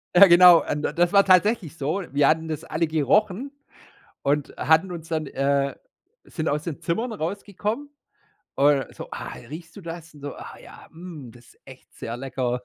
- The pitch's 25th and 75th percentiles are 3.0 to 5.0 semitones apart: Yes, average, 4.1 semitones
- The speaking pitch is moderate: Yes, medium, 160 Hz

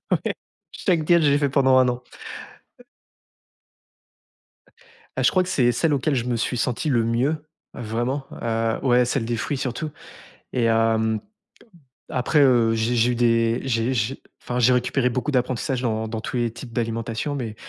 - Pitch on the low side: Yes, low, 125 Hz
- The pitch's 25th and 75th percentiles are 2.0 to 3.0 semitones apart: Yes, narrow, 2.6 semitones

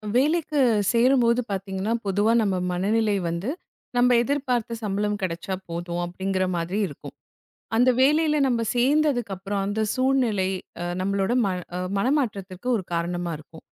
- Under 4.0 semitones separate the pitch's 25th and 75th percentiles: No, average, 4.9 semitones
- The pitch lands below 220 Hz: Yes, high, 210 Hz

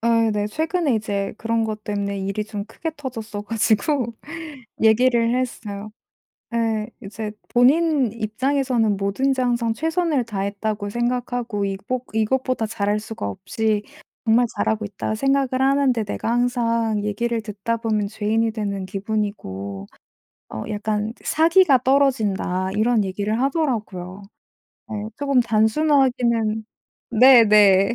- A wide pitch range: No, average, 3.3 semitones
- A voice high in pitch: Yes, high, 225 Hz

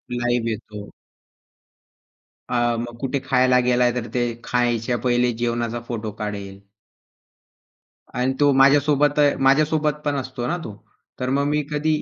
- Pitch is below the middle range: Yes, low, 125 Hz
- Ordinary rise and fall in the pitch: Yes, average, 3.1 semitones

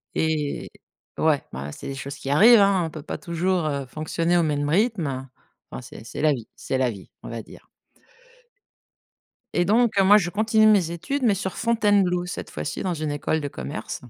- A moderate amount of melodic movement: No, wide, 5.8 semitones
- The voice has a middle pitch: Yes, medium, 165 Hz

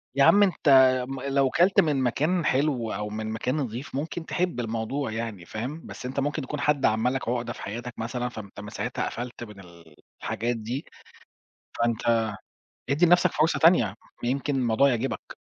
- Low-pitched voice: Yes, low, 125 Hz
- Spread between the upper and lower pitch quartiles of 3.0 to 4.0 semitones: No, average, 4.4 semitones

